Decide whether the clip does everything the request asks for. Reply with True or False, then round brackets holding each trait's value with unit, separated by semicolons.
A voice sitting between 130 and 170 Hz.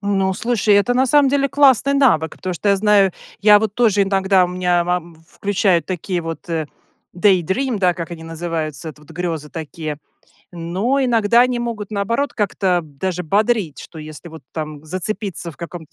False (185 Hz)